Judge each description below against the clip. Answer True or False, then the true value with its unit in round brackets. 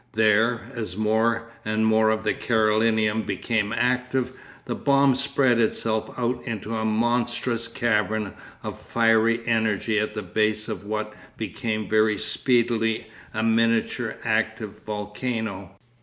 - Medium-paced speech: False (125 wpm)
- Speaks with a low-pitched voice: True (110 Hz)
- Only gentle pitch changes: True (1.5 semitones)